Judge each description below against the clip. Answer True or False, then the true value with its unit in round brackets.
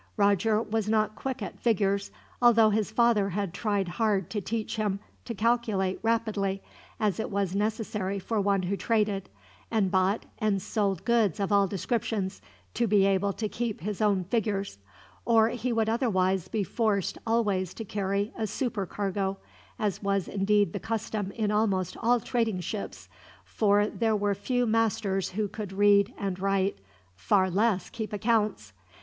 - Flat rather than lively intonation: True (2.3 semitones)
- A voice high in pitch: True (205 Hz)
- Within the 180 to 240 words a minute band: False (160 wpm)